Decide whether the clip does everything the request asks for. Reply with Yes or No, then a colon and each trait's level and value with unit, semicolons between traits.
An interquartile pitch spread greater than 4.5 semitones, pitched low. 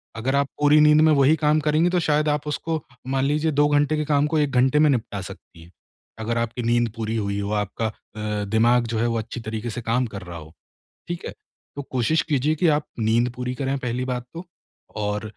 Yes: average, 5.1 semitones; low, 125 Hz